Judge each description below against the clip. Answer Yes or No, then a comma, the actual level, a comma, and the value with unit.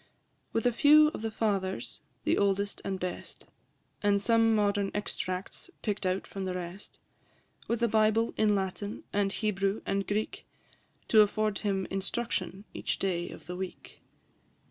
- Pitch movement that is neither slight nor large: No, narrow, 2.2 semitones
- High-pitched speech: Yes, high, 200 Hz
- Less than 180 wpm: Yes, average, 150 wpm